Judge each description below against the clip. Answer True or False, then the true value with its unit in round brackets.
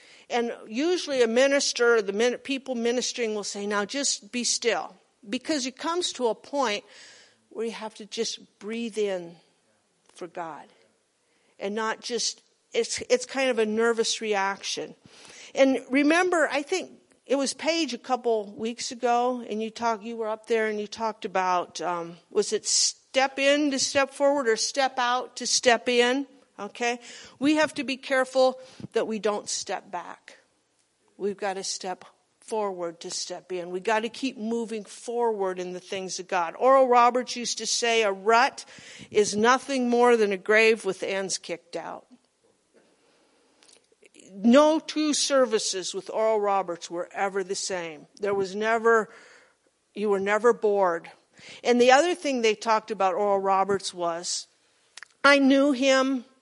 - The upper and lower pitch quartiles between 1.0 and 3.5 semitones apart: False (4.6 semitones)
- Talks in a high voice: True (230 Hz)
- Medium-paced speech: True (160 wpm)